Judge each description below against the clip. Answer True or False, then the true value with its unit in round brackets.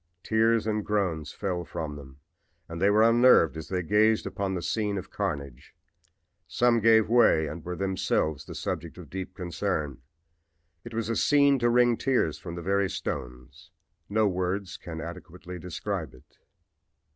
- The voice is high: False (95 Hz)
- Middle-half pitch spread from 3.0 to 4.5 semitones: False (5.2 semitones)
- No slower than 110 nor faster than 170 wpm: True (160 wpm)